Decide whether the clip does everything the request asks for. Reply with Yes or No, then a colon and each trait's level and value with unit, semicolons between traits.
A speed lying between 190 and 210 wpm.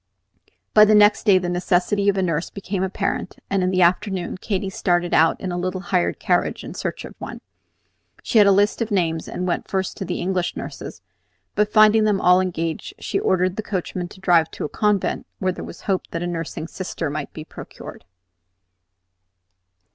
Yes: average, 195 wpm